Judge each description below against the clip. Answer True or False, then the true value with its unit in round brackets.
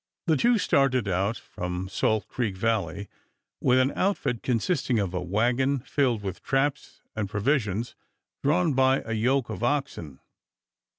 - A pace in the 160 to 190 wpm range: False (140 wpm)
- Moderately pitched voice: False (120 Hz)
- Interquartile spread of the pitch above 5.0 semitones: True (5.4 semitones)